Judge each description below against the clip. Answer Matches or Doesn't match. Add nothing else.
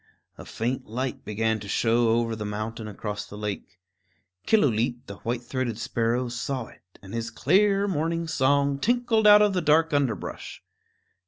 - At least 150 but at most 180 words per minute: Matches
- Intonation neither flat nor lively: Doesn't match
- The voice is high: Doesn't match